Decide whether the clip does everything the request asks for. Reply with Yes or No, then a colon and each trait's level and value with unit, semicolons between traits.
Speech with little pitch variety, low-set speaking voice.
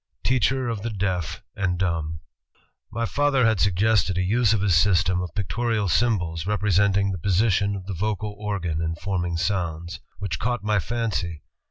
No: average, 3.5 semitones; low, 100 Hz